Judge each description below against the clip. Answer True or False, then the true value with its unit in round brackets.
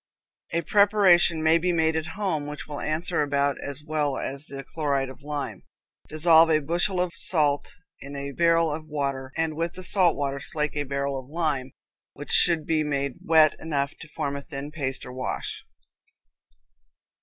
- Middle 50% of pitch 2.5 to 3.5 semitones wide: True (2.8 semitones)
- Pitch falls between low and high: True (150 Hz)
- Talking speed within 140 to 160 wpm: False (180 wpm)